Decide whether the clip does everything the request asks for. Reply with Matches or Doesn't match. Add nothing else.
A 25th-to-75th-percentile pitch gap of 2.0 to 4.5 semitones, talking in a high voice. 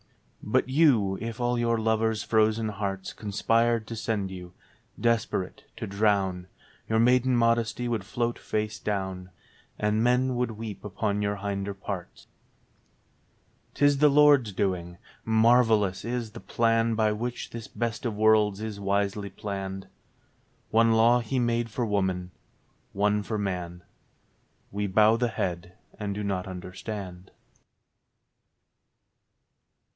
Doesn't match